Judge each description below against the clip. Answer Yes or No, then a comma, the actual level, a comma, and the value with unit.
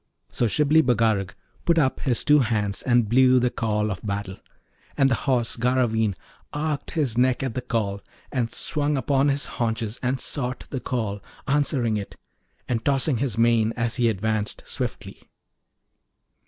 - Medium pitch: No, low, 120 Hz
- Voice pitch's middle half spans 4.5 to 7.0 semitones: No, average, 3.4 semitones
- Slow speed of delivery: No, average, 155 wpm